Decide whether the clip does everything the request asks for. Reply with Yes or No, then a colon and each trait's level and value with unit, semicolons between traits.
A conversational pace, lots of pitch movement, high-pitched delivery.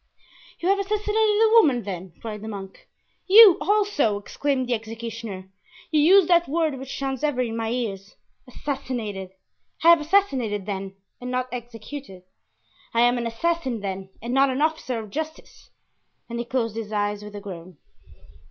Yes: average, 160 wpm; wide, 6.6 semitones; high, 245 Hz